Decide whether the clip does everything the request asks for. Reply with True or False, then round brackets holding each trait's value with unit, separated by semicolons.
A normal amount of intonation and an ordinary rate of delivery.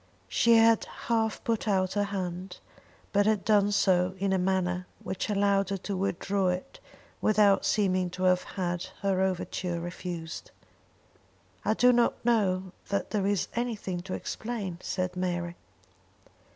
False (2.2 semitones; 145 wpm)